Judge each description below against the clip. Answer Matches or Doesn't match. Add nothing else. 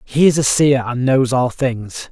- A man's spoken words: Matches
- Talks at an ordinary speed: Doesn't match